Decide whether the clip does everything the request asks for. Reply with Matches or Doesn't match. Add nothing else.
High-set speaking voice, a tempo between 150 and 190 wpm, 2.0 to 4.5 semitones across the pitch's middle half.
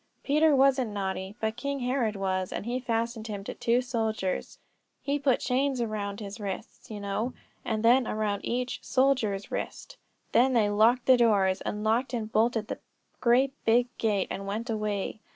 Matches